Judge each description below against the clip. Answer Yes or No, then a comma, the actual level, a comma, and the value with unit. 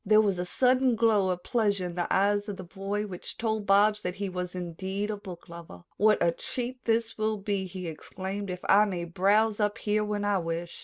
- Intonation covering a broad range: No, average, 2.8 semitones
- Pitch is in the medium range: No, high, 200 Hz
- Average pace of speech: No, fast, 215 wpm